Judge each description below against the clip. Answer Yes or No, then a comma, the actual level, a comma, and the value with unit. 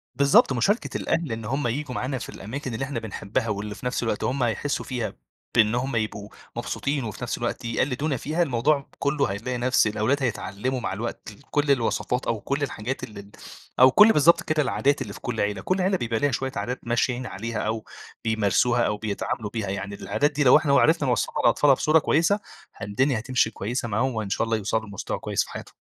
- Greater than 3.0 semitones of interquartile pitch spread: Yes, average, 4.2 semitones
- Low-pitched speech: Yes, low, 125 Hz